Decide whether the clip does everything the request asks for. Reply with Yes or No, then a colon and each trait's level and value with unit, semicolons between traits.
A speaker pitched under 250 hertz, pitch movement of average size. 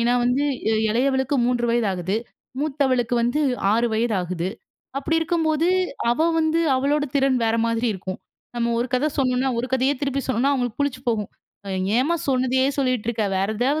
No: very high, 255 Hz; average, 3.0 semitones